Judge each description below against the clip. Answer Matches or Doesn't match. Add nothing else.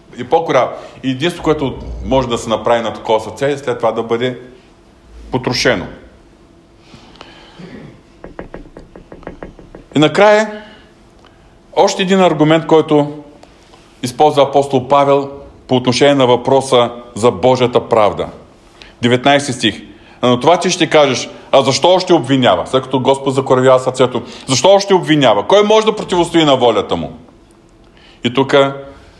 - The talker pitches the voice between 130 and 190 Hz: Matches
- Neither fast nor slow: Matches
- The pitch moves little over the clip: Doesn't match